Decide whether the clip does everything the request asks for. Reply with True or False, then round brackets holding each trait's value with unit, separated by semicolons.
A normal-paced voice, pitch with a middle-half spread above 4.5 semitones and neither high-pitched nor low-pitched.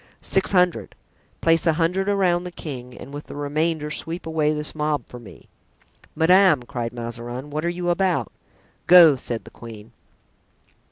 True (160 wpm; 5.4 semitones; 155 Hz)